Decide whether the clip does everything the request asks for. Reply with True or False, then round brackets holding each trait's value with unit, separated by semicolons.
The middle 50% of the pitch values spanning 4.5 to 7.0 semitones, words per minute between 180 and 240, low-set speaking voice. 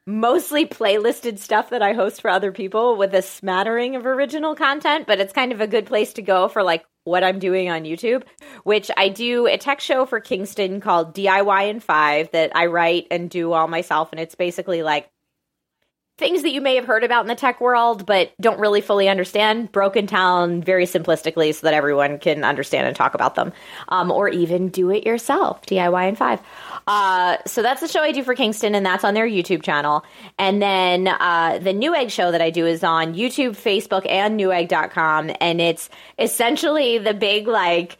False (5.2 semitones; 205 wpm; 195 Hz)